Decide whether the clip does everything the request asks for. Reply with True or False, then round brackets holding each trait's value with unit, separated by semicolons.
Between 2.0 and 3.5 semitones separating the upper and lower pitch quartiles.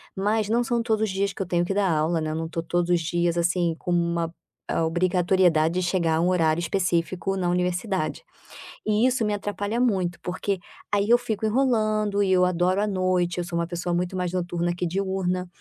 True (2.6 semitones)